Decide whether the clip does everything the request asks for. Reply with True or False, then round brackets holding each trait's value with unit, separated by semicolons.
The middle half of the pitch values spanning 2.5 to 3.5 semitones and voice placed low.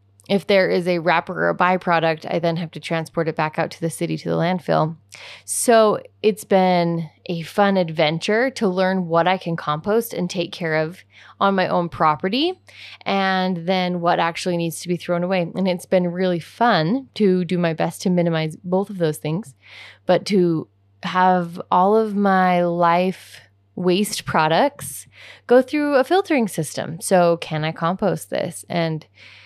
False (2.8 semitones; 175 Hz)